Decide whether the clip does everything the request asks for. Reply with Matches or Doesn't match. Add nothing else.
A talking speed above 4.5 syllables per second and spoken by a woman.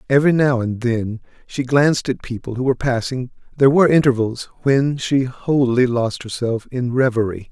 Doesn't match